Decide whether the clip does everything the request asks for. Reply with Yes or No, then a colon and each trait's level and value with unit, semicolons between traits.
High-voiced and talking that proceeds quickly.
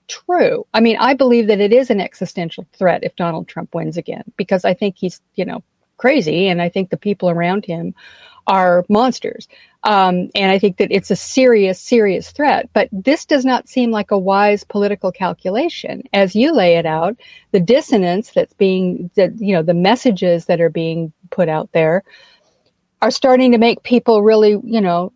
No: high, 200 Hz; average, 190 wpm